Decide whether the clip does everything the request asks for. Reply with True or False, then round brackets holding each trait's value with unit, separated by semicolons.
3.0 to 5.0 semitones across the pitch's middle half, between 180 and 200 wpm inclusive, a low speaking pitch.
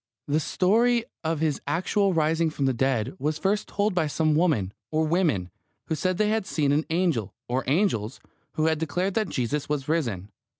False (4.7 semitones; 185 wpm; 155 Hz)